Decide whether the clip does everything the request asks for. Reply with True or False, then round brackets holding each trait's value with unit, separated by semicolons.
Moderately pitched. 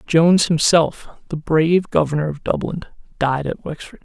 True (160 Hz)